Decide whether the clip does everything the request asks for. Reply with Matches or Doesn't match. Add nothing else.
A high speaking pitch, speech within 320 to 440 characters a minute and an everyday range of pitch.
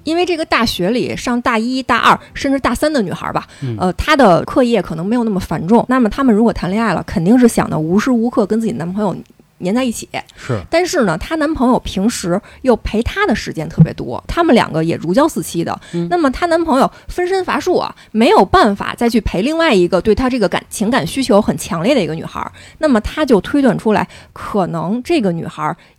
Doesn't match